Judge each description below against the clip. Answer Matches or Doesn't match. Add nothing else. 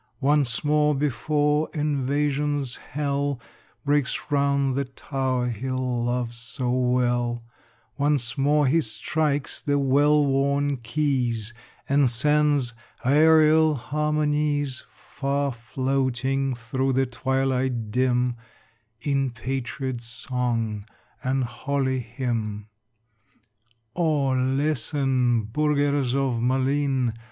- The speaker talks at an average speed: Doesn't match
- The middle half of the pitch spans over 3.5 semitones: Doesn't match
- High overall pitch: Doesn't match